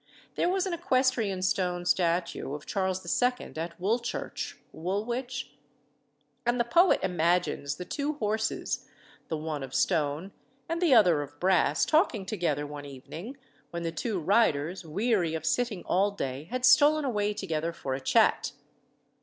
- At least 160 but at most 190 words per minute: No, average, 150 wpm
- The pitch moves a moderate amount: No, wide, 6.9 semitones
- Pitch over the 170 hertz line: Yes, high, 190 Hz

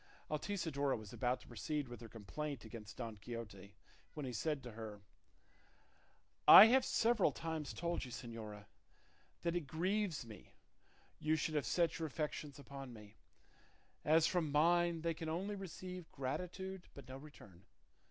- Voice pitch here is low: No, medium, 150 Hz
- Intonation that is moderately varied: No, wide, 6.4 semitones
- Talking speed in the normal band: Yes, average, 150 wpm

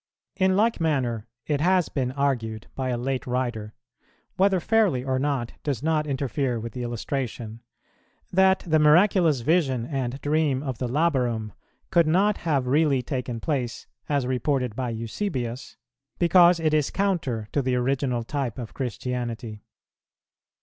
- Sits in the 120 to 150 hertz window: Yes, low, 135 Hz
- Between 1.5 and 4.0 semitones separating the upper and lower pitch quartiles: No, average, 4.5 semitones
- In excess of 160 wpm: No, average, 145 wpm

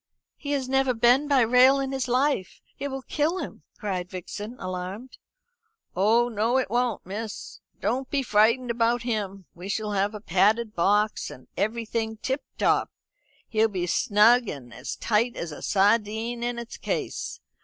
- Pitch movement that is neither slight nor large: Yes, average, 3.6 semitones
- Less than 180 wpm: Yes, average, 165 wpm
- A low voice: No, high, 225 Hz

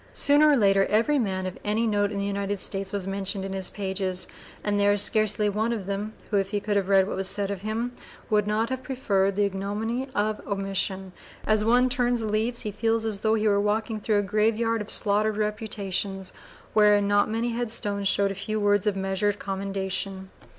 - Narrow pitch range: Yes, narrow, 1.9 semitones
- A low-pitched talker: No, high, 205 Hz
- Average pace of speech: No, fast, 210 wpm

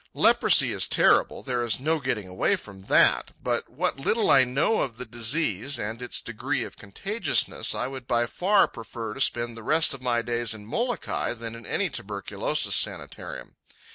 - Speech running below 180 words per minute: No, average, 185 wpm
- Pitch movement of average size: Yes, average, 3.4 semitones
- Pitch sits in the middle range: No, low, 120 Hz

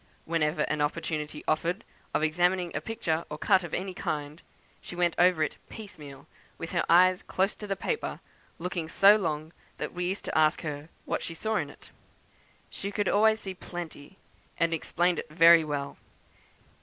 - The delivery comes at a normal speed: Yes, average, 175 wpm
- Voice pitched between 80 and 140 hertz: No, medium, 170 Hz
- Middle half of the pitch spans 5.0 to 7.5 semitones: No, average, 3.2 semitones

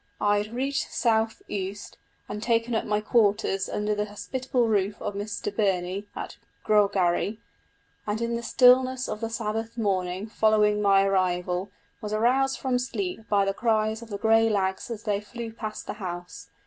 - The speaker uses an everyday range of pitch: No, narrow, 2.3 semitones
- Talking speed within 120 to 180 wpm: Yes, average, 170 wpm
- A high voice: Yes, high, 215 Hz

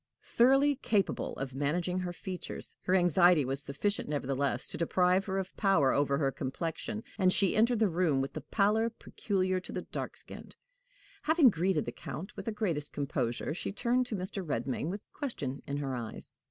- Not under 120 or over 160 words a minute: No, average, 180 wpm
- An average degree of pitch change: No, wide, 6.3 semitones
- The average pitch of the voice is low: No, medium, 180 Hz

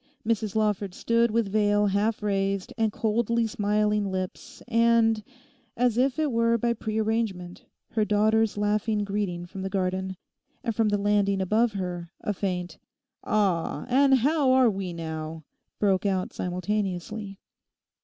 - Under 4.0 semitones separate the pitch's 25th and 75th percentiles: Yes, average, 2.9 semitones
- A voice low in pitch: No, high, 210 Hz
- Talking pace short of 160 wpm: Yes, average, 145 wpm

